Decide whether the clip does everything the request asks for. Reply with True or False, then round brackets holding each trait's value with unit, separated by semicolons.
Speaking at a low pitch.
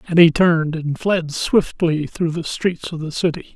False (165 Hz)